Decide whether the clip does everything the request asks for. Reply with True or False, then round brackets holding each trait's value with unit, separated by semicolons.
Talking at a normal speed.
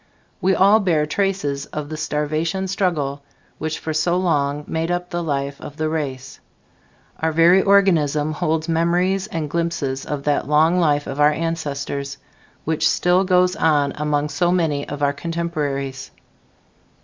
True (150 wpm)